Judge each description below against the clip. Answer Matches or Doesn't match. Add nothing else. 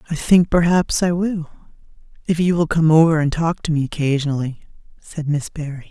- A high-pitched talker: Doesn't match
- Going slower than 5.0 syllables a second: Doesn't match